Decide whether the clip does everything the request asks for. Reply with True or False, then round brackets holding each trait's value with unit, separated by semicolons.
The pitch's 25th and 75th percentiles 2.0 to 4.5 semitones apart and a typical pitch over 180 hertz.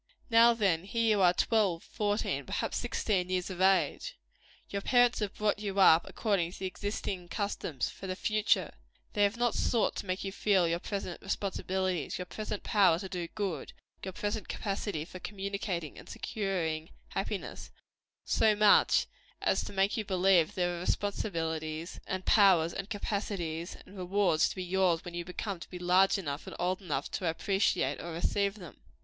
True (2.7 semitones; 190 Hz)